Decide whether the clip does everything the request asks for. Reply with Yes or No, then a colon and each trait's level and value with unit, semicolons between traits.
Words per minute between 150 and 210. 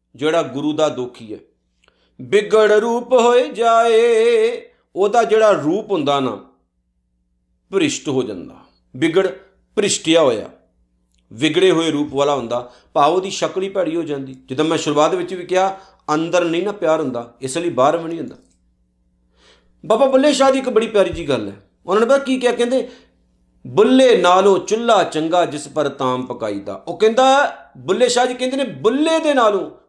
Yes: fast, 165 wpm